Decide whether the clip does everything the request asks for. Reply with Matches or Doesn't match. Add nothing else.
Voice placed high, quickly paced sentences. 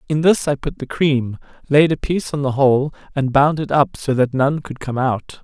Doesn't match